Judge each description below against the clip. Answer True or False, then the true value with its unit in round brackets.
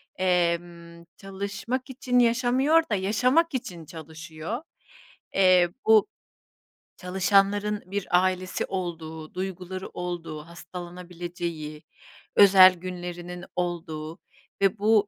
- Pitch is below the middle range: False (185 Hz)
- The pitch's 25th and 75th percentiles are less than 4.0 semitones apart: True (2.9 semitones)